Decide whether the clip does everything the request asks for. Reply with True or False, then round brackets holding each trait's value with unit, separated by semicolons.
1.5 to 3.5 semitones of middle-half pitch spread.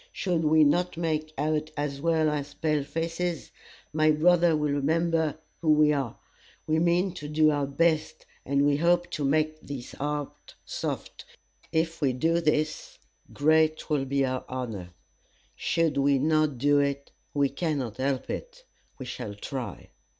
True (2.5 semitones)